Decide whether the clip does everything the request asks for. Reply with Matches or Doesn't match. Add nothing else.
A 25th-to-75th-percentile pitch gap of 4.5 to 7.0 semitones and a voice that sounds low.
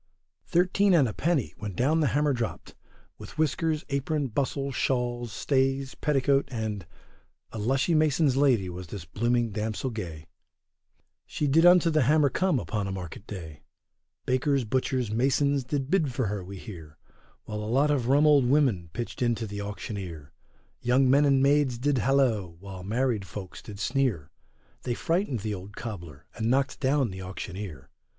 Matches